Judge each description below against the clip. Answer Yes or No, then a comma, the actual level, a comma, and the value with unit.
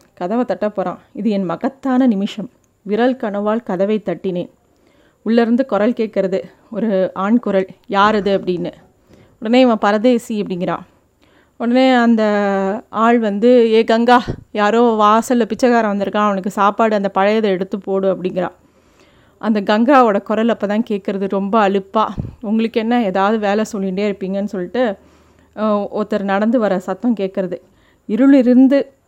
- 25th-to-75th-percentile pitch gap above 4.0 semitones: No, average, 2.9 semitones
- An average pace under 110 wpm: No, average, 125 wpm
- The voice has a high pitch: Yes, high, 210 Hz